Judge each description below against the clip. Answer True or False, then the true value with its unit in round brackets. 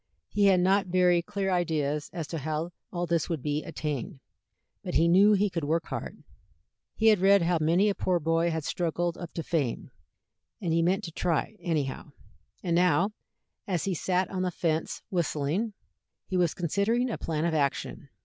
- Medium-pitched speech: True (170 Hz)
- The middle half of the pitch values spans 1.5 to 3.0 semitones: True (2.7 semitones)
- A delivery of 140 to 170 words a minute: False (190 wpm)